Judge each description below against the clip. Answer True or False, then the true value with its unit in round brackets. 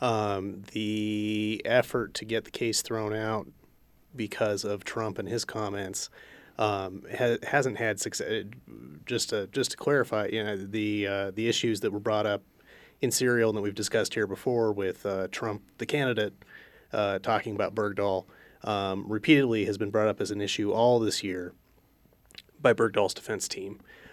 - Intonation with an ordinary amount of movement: False (1.7 semitones)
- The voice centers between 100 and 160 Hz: True (105 Hz)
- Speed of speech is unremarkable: True (170 wpm)